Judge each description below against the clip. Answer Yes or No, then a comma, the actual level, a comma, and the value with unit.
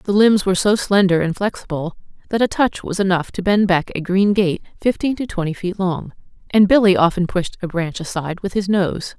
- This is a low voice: No, high, 190 Hz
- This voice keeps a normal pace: No, fast, 215 wpm